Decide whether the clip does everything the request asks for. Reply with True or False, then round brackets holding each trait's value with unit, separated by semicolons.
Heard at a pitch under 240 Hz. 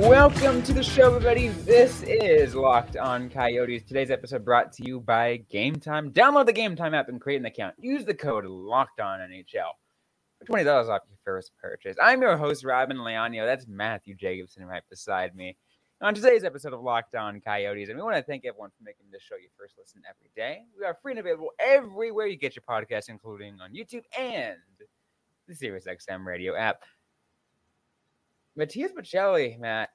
True (135 Hz)